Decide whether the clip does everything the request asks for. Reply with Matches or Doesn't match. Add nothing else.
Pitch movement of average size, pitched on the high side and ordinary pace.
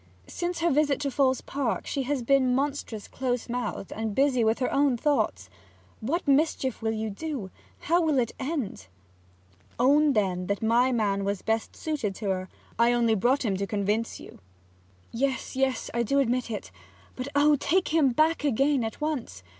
Matches